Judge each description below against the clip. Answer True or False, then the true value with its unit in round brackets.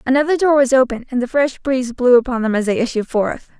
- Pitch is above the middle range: True (255 Hz)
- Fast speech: True (250 wpm)